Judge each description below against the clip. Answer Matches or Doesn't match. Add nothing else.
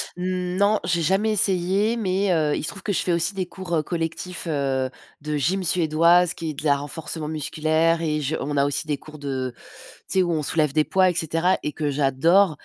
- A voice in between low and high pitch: Matches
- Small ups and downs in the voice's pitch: Doesn't match